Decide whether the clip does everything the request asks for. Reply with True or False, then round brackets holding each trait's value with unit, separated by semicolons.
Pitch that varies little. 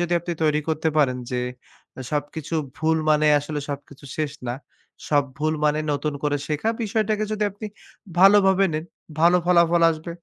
False (3.2 semitones)